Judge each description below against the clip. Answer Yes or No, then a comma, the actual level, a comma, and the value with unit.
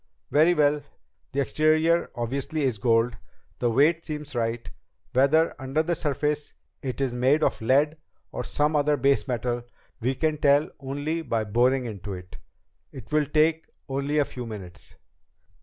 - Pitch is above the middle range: No, medium, 140 Hz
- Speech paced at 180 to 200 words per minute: No, average, 155 wpm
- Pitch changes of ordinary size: Yes, average, 3.9 semitones